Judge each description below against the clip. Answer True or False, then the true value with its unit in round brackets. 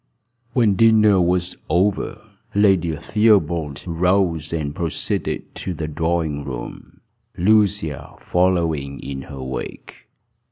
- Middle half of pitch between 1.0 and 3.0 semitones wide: False (3.9 semitones)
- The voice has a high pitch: False (85 Hz)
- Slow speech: True (105 wpm)